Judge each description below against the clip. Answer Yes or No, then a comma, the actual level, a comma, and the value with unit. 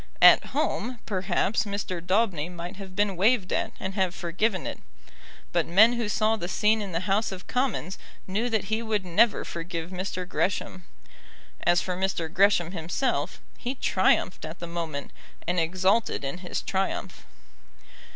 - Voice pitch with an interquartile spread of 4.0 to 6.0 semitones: No, average, 3.3 semitones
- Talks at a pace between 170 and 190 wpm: No, average, 160 wpm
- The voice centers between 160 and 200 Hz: Yes, high, 190 Hz